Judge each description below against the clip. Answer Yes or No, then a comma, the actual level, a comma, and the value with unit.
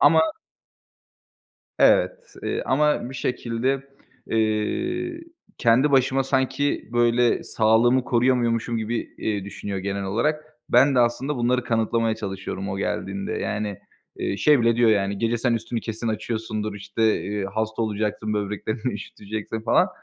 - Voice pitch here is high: No, low, 115 Hz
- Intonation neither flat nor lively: Yes, average, 3.2 semitones